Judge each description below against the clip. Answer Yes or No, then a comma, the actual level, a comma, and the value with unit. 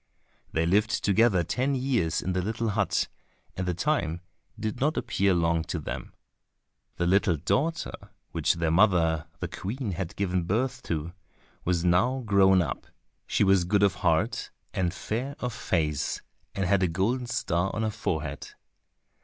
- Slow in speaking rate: No, average, 160 wpm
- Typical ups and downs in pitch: Yes, average, 4.5 semitones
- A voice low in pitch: Yes, very low, 95 Hz